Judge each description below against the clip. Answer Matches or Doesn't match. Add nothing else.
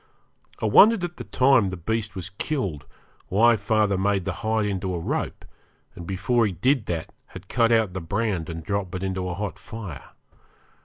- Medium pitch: Doesn't match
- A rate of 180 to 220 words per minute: Matches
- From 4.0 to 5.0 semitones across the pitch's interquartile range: Doesn't match